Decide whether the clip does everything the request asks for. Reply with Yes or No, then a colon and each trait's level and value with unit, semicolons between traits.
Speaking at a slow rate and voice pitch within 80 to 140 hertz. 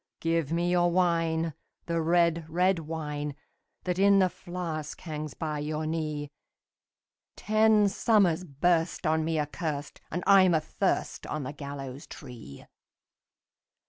No: slow, 125 wpm; medium, 165 Hz